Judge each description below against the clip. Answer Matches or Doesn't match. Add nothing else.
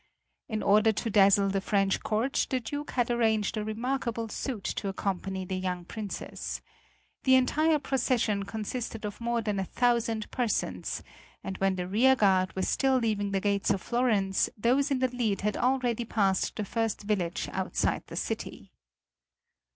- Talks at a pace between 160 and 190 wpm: Matches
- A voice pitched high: Matches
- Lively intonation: Doesn't match